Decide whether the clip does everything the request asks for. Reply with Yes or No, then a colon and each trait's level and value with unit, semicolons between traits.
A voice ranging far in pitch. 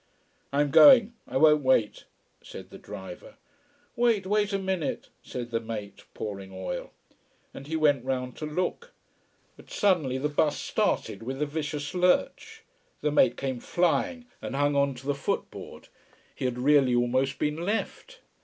Yes: wide, 6.0 semitones